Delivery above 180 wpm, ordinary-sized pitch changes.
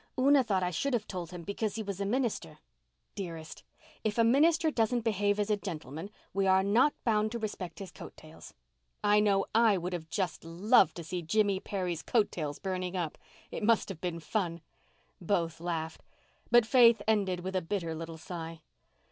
Yes: average, 190 wpm; average, 4.3 semitones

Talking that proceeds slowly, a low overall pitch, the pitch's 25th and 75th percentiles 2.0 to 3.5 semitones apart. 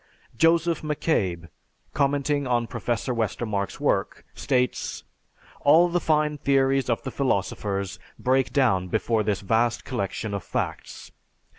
No: slow, 120 wpm; low, 125 Hz; average, 4.9 semitones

